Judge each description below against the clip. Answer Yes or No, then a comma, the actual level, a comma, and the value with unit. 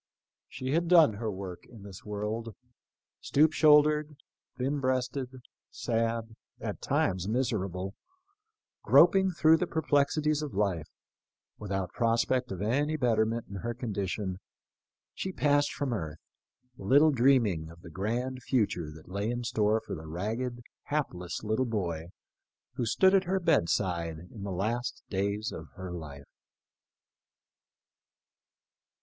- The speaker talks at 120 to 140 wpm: Yes, slow, 135 wpm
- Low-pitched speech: Yes, low, 115 Hz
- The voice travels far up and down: Yes, wide, 6.4 semitones